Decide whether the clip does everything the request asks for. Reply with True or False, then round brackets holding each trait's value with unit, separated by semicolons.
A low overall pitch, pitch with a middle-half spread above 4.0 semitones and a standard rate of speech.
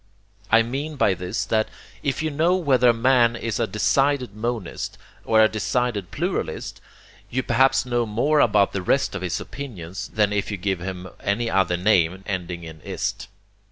True (110 Hz; 4.5 semitones; 175 wpm)